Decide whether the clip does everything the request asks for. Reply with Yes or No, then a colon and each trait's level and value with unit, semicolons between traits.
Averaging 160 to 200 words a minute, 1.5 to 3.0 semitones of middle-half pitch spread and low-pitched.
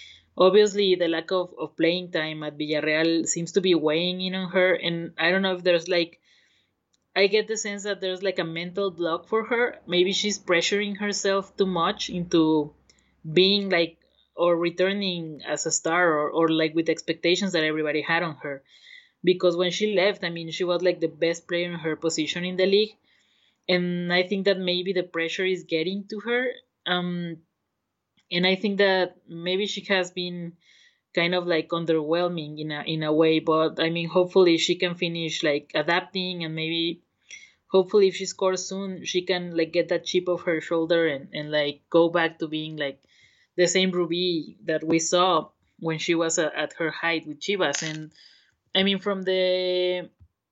No: average, 190 wpm; narrow, 2.4 semitones; medium, 175 Hz